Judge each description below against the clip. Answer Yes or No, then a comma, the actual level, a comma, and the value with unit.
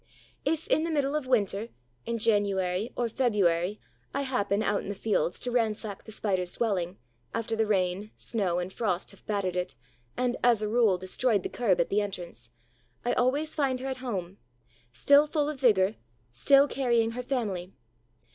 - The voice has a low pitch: No, high, 215 Hz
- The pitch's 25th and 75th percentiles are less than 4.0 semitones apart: No, average, 4.8 semitones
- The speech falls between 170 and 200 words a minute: Yes, average, 175 wpm